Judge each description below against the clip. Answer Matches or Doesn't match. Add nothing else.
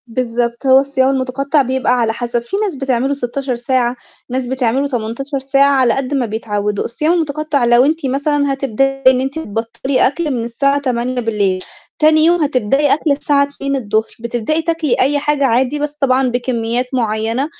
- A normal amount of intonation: Matches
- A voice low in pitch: Doesn't match